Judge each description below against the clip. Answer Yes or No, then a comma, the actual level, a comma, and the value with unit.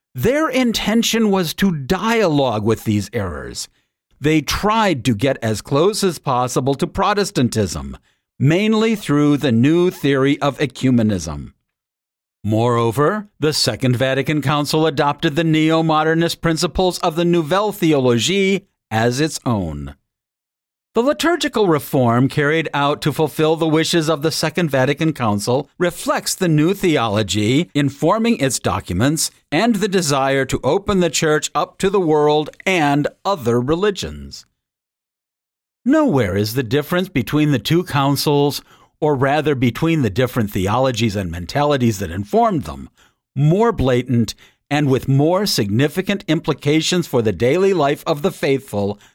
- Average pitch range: No, wide, 5.8 semitones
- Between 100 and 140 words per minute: Yes, slow, 135 wpm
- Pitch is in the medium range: Yes, medium, 150 Hz